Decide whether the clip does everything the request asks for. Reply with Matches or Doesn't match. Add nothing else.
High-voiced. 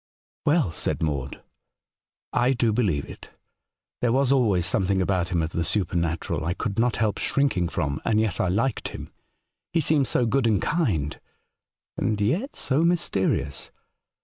Doesn't match